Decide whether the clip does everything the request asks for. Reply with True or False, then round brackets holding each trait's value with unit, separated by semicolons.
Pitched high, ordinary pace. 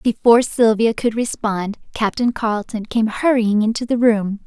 True (225 Hz; 150 wpm)